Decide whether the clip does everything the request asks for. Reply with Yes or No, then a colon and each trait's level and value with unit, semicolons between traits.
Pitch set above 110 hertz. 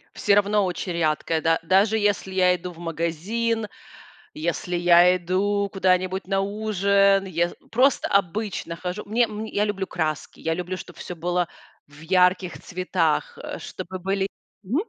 Yes: medium, 185 Hz